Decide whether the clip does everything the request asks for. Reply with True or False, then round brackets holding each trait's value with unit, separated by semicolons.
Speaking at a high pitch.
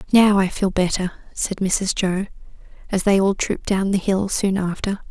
True (195 Hz)